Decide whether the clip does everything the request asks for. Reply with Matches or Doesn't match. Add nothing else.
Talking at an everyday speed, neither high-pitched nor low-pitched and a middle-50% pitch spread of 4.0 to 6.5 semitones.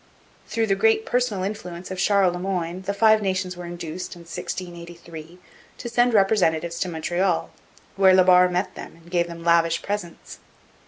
Doesn't match